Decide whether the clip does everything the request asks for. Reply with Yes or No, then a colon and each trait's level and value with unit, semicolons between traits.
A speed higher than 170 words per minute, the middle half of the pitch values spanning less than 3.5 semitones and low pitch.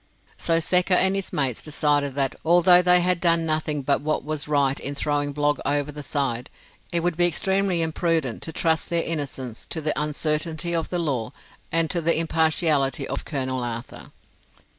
No: average, 180 wpm; average, 3.0 semitones; medium, 155 Hz